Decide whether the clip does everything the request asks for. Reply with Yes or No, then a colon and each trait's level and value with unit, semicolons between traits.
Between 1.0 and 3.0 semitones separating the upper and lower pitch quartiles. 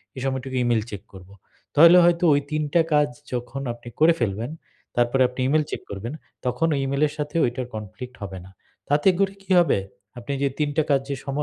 No: average, 3.8 semitones